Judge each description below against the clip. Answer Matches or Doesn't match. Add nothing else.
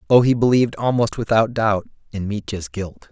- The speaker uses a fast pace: Doesn't match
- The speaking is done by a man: Matches